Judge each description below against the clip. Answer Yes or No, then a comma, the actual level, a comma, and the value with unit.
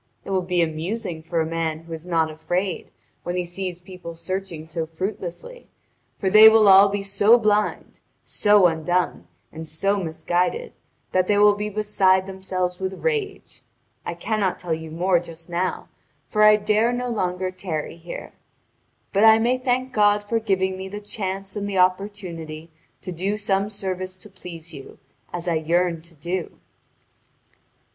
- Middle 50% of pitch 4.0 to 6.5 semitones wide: No, average, 3.4 semitones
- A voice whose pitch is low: No, medium, 185 Hz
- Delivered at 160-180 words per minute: Yes, average, 165 wpm